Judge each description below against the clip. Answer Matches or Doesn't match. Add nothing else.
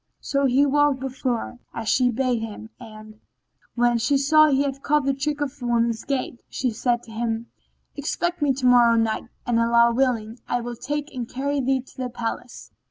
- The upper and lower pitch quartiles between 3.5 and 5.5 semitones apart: Doesn't match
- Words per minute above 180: Matches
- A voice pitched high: Matches